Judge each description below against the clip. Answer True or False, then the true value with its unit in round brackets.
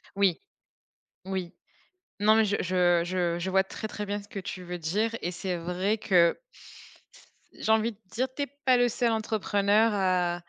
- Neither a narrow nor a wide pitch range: True (3.5 semitones)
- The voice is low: False (195 Hz)